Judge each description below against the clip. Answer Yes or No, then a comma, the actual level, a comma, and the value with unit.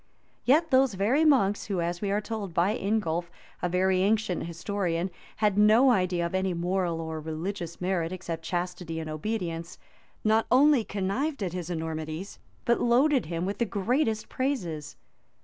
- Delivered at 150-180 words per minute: Yes, average, 160 wpm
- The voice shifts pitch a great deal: No, average, 4.4 semitones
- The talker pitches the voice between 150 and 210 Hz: Yes, high, 190 Hz